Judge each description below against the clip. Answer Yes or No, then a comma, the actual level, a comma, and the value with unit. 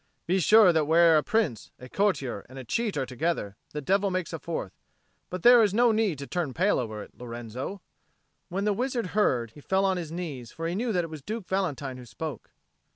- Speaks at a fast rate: Yes, fast, 220 wpm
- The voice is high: No, medium, 170 Hz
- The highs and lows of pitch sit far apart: Yes, wide, 6.9 semitones